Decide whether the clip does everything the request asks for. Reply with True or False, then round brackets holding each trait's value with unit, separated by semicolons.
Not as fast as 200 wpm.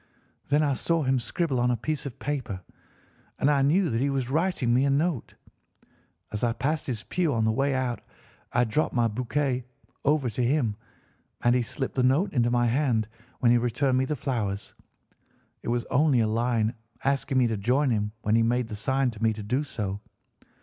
False (205 wpm)